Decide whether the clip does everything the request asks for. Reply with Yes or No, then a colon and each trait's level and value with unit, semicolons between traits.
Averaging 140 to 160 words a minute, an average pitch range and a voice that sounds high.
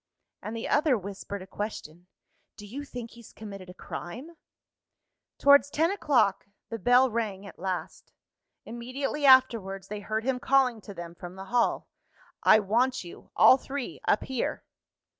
Yes: average, 155 wpm; average, 4.9 semitones; high, 225 Hz